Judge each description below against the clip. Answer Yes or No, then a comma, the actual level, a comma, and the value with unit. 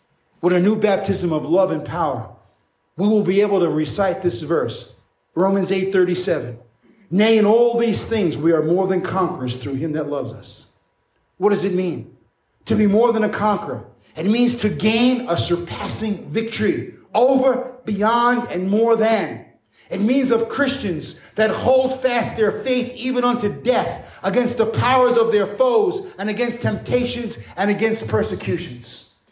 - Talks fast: No, average, 165 wpm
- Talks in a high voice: Yes, high, 210 Hz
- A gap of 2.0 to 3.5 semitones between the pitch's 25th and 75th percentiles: No, average, 4.8 semitones